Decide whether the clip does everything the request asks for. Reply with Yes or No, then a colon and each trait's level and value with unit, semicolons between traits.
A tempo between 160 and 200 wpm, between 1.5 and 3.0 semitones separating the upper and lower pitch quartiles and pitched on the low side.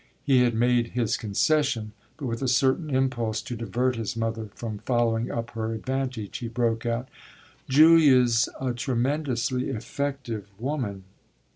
No: average, 140 wpm; average, 2.7 semitones; low, 120 Hz